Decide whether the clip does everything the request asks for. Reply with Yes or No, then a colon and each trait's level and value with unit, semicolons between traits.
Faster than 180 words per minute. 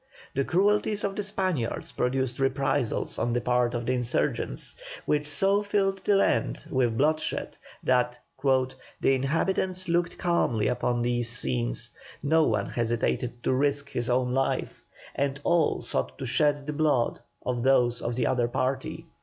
No: average, 155 wpm